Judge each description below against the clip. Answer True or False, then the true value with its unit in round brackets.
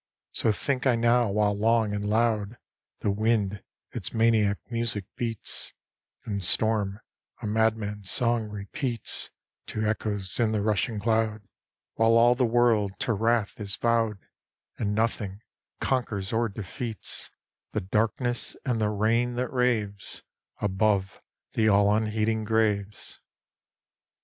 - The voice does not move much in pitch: True (2.1 semitones)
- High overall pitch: False (110 Hz)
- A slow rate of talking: True (125 wpm)